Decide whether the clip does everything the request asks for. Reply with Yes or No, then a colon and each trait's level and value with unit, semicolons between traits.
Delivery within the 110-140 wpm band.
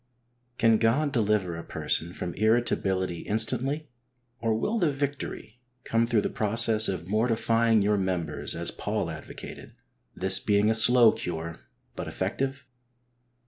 Yes: slow, 135 wpm